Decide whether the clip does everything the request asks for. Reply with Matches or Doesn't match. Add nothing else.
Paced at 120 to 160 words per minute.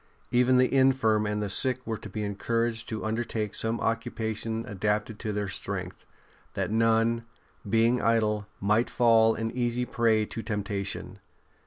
Matches